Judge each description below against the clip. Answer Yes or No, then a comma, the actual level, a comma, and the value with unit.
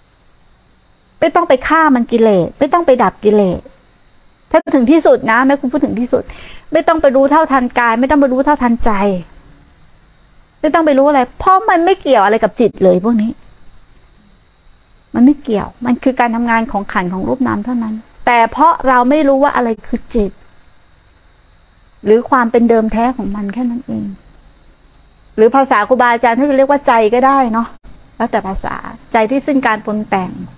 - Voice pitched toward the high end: Yes, high, 240 Hz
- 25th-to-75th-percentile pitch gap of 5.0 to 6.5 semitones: No, average, 4.1 semitones